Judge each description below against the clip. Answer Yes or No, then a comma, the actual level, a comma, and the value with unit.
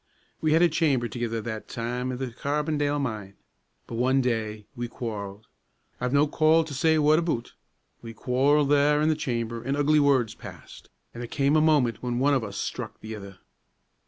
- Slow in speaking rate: No, average, 190 wpm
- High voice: No, low, 130 Hz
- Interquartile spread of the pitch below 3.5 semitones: No, average, 4.2 semitones